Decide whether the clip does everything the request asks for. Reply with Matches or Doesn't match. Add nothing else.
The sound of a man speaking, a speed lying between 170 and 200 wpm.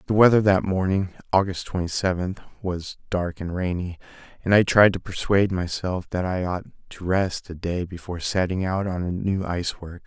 Matches